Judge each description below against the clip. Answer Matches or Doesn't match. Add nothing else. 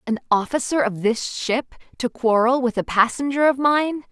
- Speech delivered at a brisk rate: Doesn't match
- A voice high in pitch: Matches